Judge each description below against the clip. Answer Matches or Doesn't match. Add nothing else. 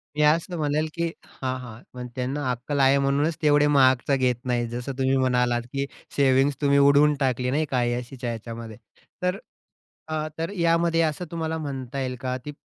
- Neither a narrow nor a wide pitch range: Matches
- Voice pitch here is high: Doesn't match